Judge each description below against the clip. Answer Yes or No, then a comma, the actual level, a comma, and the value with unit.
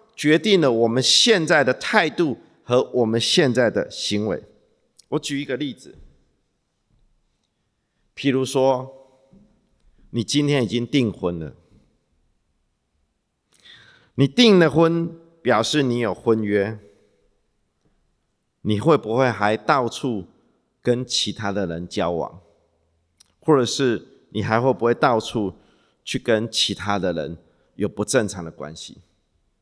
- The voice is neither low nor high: No, low, 120 Hz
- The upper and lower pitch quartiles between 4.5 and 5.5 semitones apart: Yes, average, 5.1 semitones